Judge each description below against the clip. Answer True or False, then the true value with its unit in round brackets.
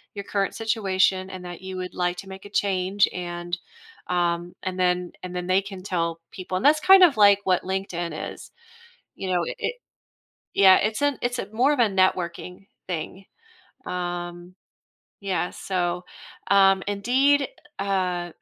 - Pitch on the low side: False (185 Hz)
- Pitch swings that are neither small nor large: False (2.0 semitones)